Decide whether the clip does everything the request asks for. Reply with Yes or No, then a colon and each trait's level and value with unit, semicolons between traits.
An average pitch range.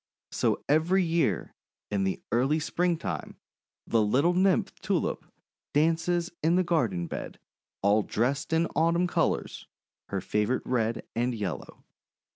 No: wide, 7.6 semitones